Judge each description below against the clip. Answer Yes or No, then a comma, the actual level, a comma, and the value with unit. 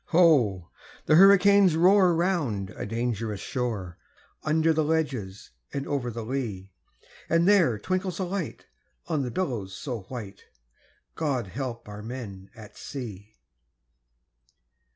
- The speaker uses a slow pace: Yes, slow, 125 wpm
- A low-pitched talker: Yes, low, 130 Hz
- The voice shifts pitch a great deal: Yes, wide, 7.8 semitones